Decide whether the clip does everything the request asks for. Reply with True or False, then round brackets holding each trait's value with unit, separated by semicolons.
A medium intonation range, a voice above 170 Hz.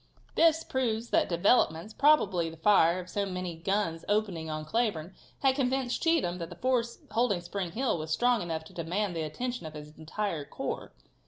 False (6.6 semitones; 190 Hz)